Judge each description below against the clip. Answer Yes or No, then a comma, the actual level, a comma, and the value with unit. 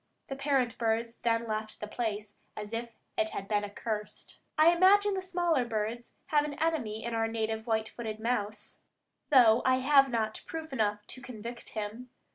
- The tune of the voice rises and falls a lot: No, average, 3.8 semitones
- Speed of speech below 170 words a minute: No, average, 175 wpm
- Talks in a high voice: Yes, high, 230 Hz